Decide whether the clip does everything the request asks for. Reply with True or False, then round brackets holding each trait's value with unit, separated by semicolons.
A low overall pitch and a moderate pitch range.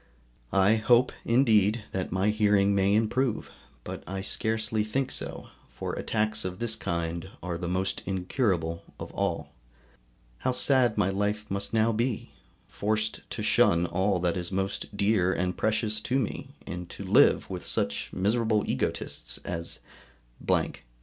True (105 Hz; 3.0 semitones)